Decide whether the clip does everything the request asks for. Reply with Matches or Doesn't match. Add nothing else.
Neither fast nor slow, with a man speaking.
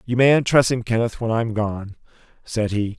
Doesn't match